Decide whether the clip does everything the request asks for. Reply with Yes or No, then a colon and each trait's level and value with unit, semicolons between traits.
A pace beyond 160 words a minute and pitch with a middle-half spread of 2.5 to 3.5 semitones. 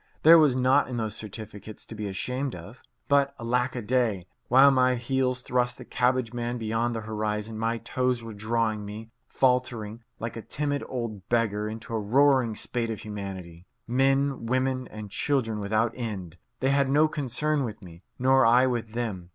Yes: average, 175 wpm; average, 3.0 semitones